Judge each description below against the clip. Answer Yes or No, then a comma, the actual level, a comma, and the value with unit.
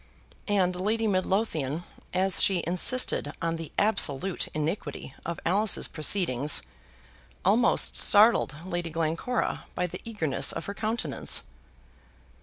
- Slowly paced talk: Yes, slow, 110 wpm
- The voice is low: No, medium, 180 Hz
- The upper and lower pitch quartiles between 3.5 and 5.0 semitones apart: Yes, average, 4.2 semitones